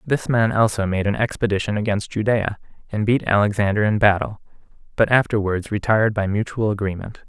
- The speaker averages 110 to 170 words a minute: Yes, average, 155 wpm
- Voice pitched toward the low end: Yes, low, 105 Hz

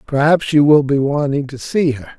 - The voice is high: No, medium, 145 Hz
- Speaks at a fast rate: Yes, fast, 220 wpm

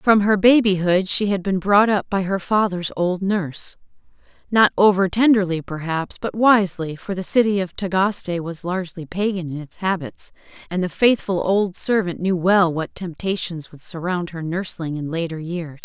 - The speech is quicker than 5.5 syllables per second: No, 4.8 syllables/s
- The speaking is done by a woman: Yes, female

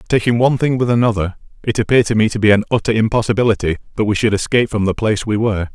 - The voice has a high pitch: No, low, 110 Hz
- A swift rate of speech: Yes, fast, 240 wpm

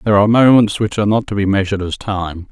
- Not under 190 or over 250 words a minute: No, fast, 265 wpm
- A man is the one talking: Yes, male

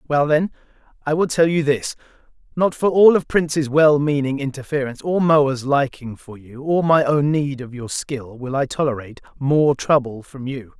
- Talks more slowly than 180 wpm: No, average, 190 wpm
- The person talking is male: Yes, male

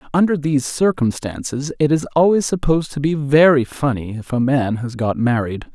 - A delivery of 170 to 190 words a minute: Yes, average, 180 wpm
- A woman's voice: No, male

